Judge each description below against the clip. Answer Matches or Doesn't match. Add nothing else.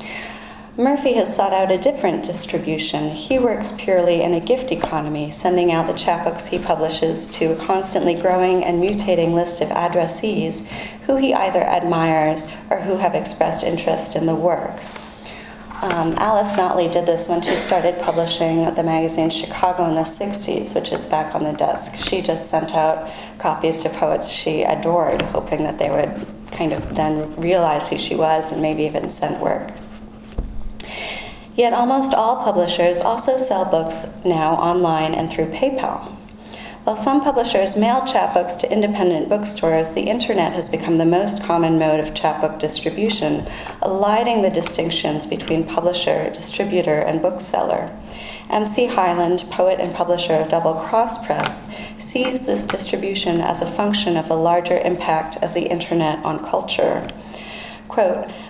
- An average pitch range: Matches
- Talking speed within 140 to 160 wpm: Matches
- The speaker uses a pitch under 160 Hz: Doesn't match